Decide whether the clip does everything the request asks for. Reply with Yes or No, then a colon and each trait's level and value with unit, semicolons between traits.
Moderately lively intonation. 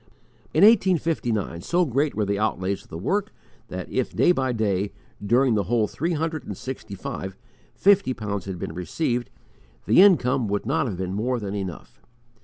No: wide, 7.8 semitones